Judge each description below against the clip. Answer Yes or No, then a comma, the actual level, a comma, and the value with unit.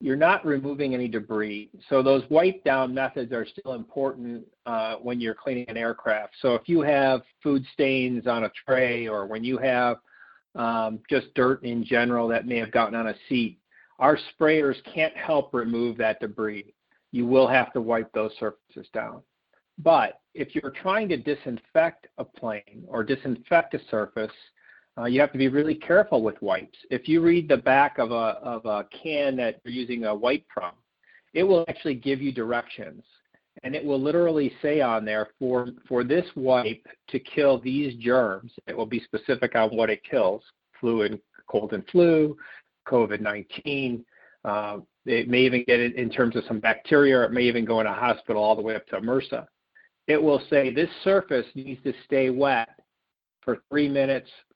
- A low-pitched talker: Yes, low, 125 Hz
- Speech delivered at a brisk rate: No, average, 185 wpm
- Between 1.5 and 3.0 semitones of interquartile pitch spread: No, average, 3.4 semitones